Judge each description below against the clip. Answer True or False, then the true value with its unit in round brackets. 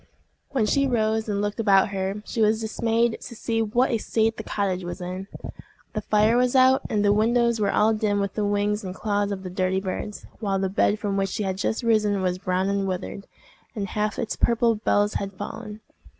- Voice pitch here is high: True (210 Hz)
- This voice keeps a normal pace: False (215 wpm)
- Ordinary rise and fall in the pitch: False (2.2 semitones)